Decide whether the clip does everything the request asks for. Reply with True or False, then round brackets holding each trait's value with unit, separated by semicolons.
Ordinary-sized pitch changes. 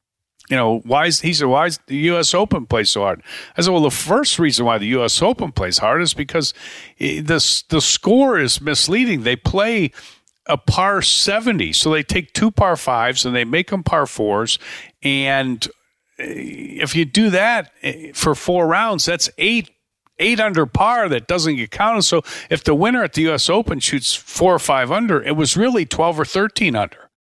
False (6.3 semitones)